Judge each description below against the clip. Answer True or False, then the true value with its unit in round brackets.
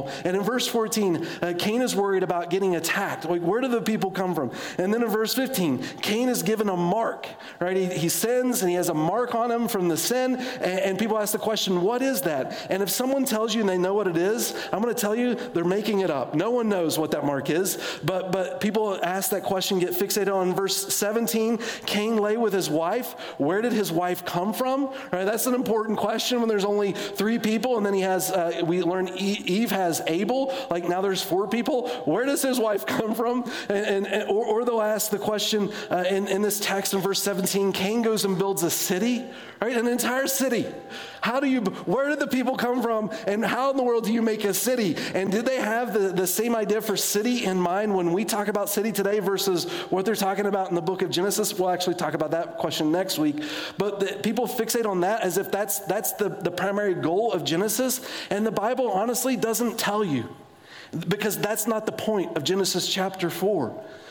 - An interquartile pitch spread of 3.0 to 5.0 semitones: True (3.4 semitones)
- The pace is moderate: False (235 wpm)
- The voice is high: True (205 Hz)